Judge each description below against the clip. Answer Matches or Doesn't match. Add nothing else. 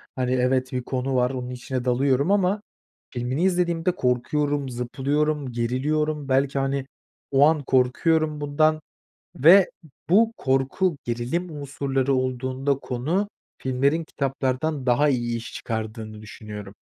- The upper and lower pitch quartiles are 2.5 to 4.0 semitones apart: Matches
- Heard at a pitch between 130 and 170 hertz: Matches